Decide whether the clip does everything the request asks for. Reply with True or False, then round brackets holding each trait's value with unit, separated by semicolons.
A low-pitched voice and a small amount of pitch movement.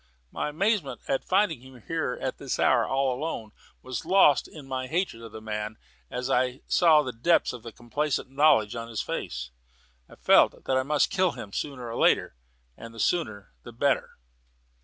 False (130 Hz; 4.8 semitones)